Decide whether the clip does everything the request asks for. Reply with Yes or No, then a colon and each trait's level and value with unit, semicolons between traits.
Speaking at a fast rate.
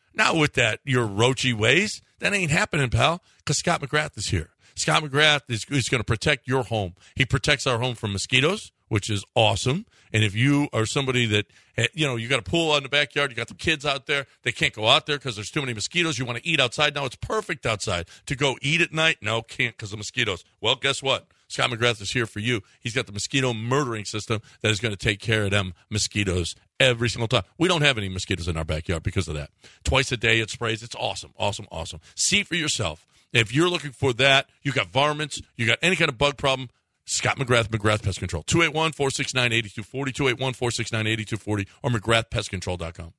Yes: fast, 220 wpm